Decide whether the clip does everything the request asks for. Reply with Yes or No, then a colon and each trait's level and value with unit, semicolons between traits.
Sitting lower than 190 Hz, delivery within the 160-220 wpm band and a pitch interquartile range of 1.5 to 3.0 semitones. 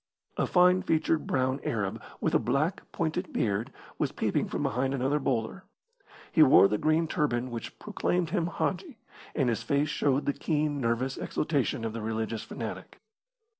No: medium, 140 Hz; average, 165 wpm; wide, 5.5 semitones